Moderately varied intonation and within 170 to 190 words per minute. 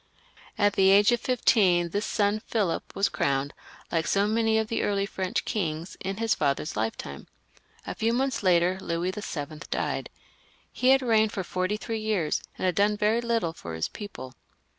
Yes: average, 4.4 semitones; average, 180 wpm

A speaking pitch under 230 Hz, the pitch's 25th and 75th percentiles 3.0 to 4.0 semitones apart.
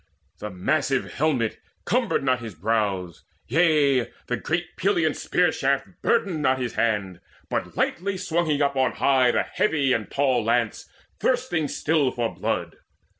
No: low, 135 Hz; wide, 5.6 semitones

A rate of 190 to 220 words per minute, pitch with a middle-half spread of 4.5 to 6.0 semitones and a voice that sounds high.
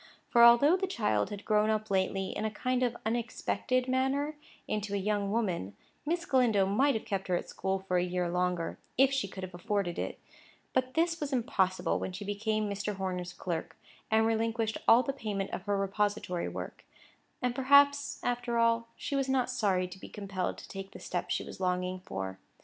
Yes: average, 195 wpm; average, 4.8 semitones; high, 210 Hz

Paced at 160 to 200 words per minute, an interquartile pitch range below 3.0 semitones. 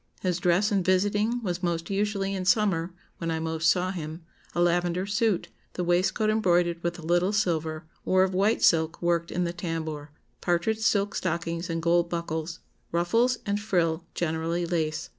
Yes: average, 170 wpm; narrow, 2.6 semitones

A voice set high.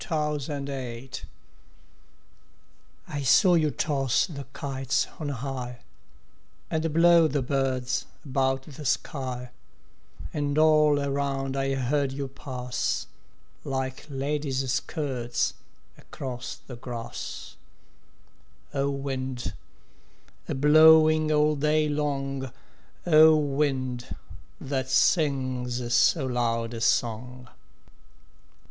No: low, 135 Hz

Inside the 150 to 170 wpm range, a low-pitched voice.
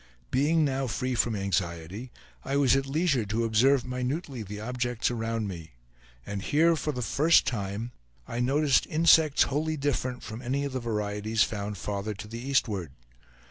Yes: average, 165 wpm; low, 120 Hz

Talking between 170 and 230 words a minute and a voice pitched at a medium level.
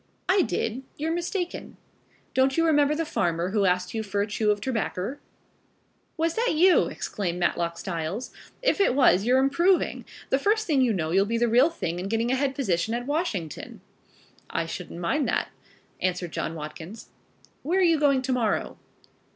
No: average, 180 wpm; high, 240 Hz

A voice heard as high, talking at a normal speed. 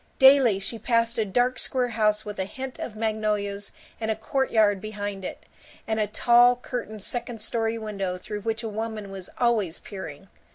Yes: high, 220 Hz; average, 175 wpm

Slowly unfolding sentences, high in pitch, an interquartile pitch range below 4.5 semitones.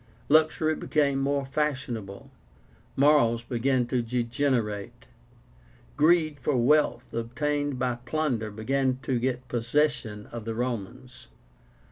No: slow, 105 wpm; low, 130 Hz; average, 3.6 semitones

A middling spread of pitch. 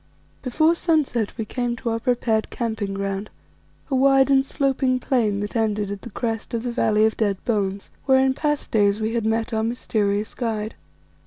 Yes: average, 3.4 semitones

